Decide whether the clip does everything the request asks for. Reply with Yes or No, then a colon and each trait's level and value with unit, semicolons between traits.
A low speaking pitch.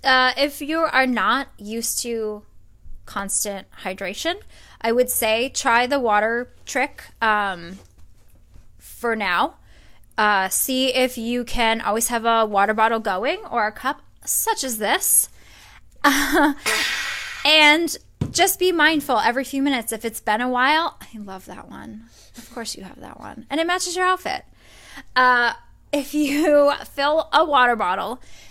No: high, 235 Hz